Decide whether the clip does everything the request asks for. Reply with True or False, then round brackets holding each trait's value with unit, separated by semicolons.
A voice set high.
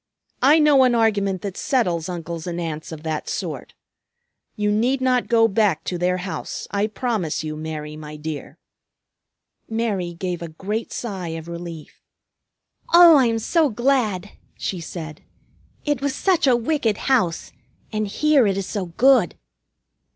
True (200 Hz)